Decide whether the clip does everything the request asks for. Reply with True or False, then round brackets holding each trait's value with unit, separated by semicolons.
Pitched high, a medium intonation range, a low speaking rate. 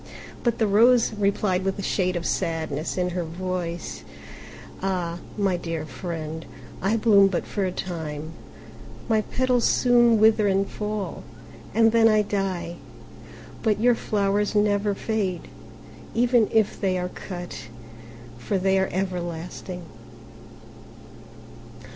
True (195 Hz; 3.4 semitones; 125 wpm)